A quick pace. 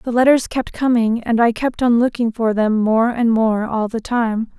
Yes: fast, 225 wpm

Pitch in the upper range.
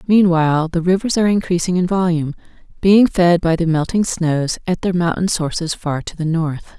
No: medium, 175 Hz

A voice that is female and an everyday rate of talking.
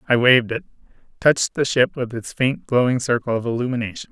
No: male; average, 190 wpm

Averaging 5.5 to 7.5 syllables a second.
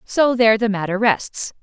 No: 4.8 syllables/s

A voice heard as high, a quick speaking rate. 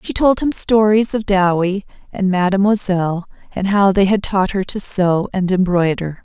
No: high, 195 Hz; average, 175 wpm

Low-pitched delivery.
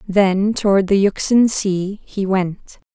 No: high, 195 Hz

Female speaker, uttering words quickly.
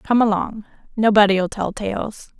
No: female; slow, 125 wpm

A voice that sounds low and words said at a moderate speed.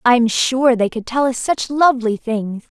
No: high, 240 Hz; average, 195 wpm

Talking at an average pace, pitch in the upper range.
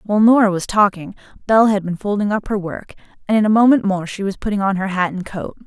No: fast, 255 wpm; high, 200 Hz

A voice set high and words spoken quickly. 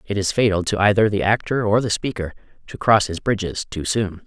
No: low, 105 Hz; fast, 225 wpm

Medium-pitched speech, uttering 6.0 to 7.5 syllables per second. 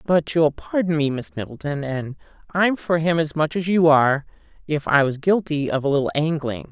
No: medium, 155 Hz; 5.2 syllables/s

